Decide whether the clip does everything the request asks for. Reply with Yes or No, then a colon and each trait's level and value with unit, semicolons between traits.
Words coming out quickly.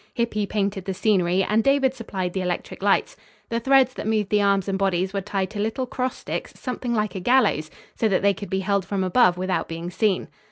Yes: fast, 225 wpm